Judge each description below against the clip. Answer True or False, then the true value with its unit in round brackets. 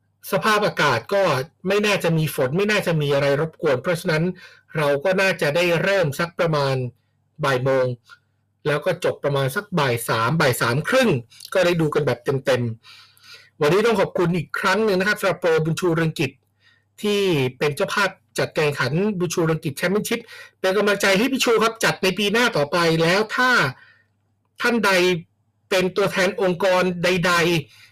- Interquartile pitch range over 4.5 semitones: True (5.2 semitones)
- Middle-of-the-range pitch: True (175 Hz)